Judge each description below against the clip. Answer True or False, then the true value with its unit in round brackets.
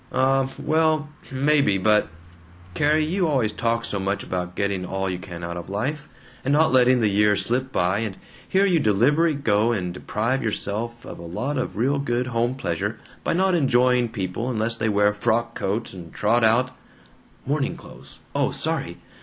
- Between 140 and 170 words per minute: False (180 wpm)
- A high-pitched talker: False (115 Hz)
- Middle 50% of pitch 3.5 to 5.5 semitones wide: True (5.0 semitones)